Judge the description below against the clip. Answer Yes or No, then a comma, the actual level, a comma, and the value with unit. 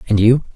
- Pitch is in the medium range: No, low, 115 Hz